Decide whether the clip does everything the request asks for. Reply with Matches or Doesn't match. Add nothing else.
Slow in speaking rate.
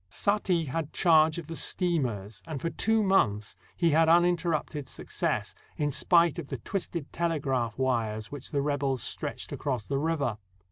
Doesn't match